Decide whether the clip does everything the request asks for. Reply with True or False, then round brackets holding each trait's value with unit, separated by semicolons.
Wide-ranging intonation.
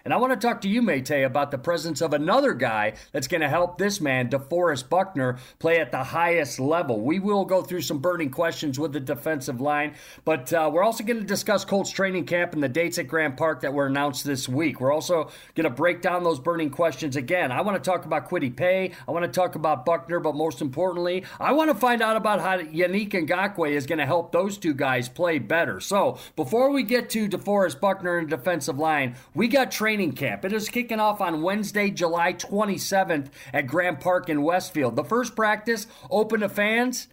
False (4.3 semitones)